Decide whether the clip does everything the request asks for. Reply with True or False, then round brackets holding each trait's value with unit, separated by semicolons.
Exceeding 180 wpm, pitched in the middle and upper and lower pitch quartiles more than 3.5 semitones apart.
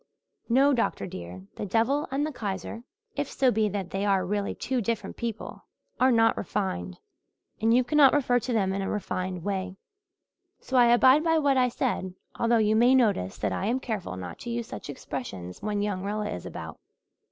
False (195 wpm; 215 Hz; 4.7 semitones)